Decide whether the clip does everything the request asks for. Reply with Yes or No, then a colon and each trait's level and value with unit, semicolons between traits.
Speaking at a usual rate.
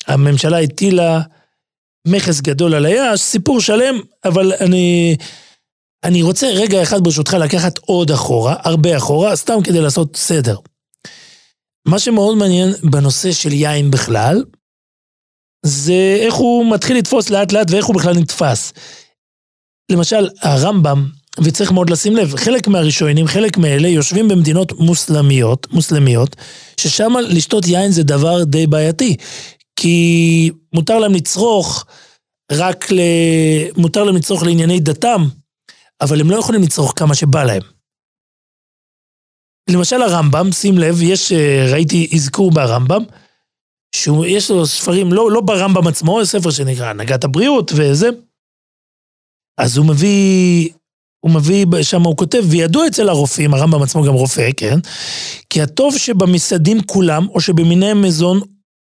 Yes: average, 125 wpm